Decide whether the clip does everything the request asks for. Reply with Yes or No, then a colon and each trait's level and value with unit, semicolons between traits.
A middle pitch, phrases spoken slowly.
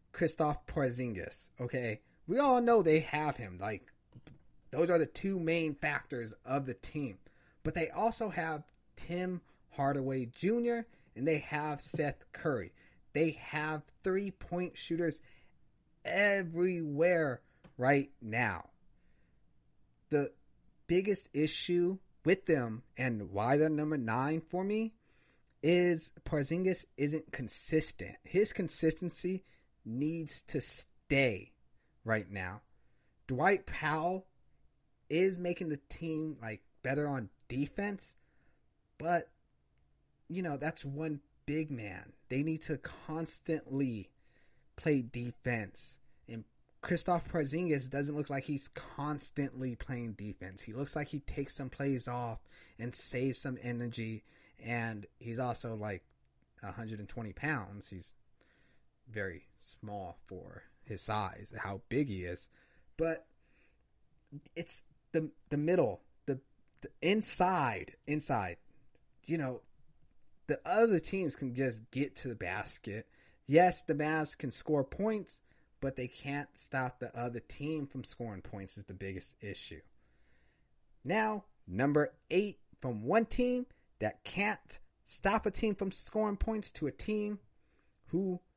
Yes: medium, 145 Hz; slow, 120 wpm